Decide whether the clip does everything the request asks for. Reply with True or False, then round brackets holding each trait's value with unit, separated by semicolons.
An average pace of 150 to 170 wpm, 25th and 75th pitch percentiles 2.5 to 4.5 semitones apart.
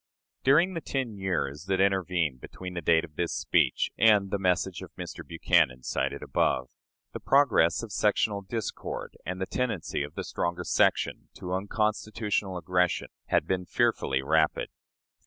True (155 wpm; 4.0 semitones)